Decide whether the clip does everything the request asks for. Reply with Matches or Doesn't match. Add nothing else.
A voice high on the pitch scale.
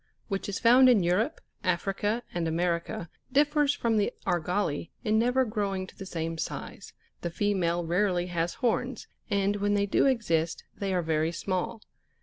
Matches